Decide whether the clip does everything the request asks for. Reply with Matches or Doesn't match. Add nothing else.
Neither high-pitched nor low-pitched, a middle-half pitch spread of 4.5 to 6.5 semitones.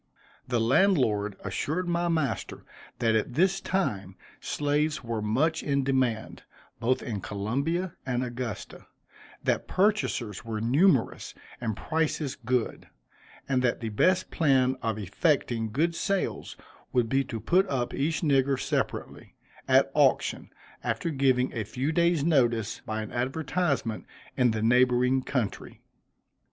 Doesn't match